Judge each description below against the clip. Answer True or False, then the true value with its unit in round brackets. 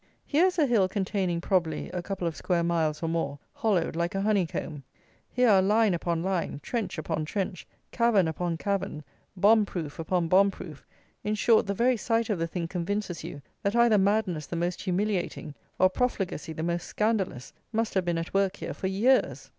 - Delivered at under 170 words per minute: False (190 wpm)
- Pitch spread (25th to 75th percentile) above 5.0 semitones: False (3.9 semitones)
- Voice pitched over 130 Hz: True (185 Hz)